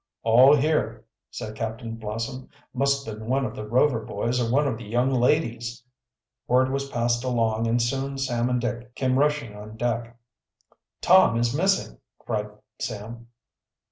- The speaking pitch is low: Yes, low, 120 Hz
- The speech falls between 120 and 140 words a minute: No, average, 160 wpm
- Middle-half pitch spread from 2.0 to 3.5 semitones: Yes, average, 2.7 semitones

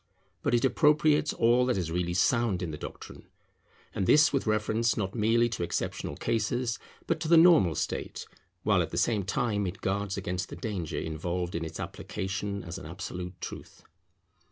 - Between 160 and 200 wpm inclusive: Yes, average, 180 wpm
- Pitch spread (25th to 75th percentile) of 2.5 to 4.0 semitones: No, average, 5.0 semitones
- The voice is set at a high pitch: No, low, 100 Hz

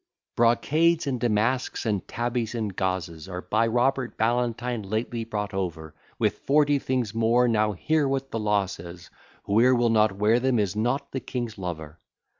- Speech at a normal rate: Yes, average, 165 wpm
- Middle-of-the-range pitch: No, low, 115 Hz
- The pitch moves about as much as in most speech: Yes, average, 3.7 semitones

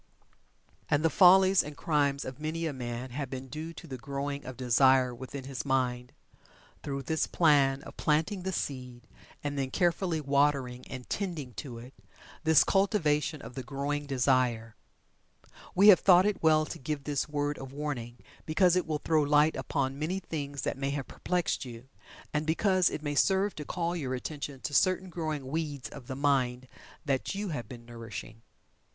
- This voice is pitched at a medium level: Yes, medium, 145 Hz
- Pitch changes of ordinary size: Yes, average, 3.5 semitones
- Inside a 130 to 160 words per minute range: No, average, 180 wpm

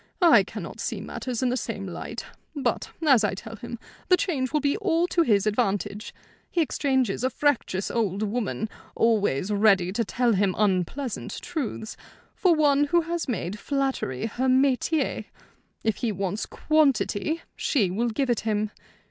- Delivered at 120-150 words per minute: No, average, 160 wpm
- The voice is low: No, high, 235 Hz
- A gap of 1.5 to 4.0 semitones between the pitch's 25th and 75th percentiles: No, wide, 5.5 semitones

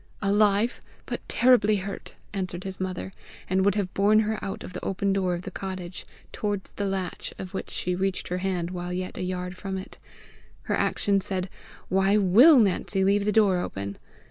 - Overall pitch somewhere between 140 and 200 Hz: Yes, high, 190 Hz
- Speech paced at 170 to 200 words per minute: Yes, average, 190 wpm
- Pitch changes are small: Yes, narrow, 1.7 semitones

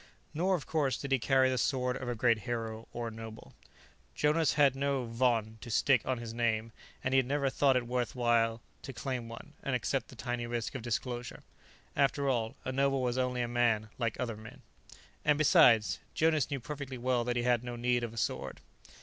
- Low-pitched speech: Yes, low, 125 Hz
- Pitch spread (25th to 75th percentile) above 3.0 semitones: No, narrow, 2.5 semitones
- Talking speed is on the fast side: Yes, fast, 215 wpm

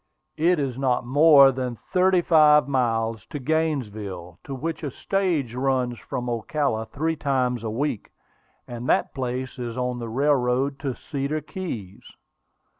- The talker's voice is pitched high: No, low, 130 Hz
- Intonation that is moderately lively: Yes, average, 3.7 semitones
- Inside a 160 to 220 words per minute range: No, average, 145 wpm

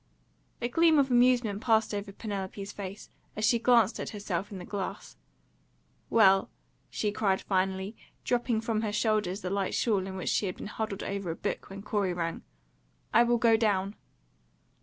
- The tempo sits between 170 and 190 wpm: Yes, average, 175 wpm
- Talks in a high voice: Yes, high, 205 Hz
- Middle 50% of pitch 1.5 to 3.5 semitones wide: Yes, average, 2.8 semitones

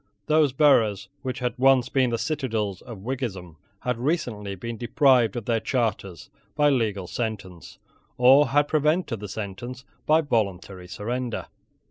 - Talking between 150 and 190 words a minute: No, average, 140 wpm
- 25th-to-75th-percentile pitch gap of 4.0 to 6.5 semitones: Yes, average, 4.6 semitones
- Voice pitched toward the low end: Yes, low, 120 Hz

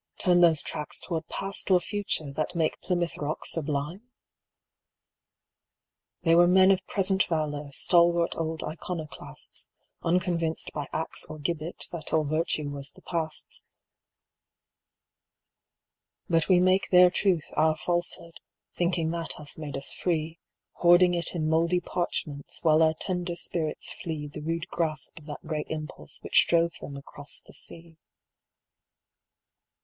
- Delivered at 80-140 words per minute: Yes, slow, 135 wpm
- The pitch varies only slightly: Yes, narrow, 2.2 semitones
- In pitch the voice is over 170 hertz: No, medium, 165 Hz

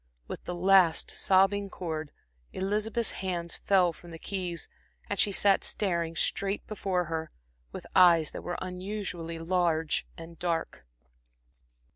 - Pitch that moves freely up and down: No, average, 2.8 semitones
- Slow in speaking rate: Yes, slow, 130 wpm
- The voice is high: No, medium, 180 Hz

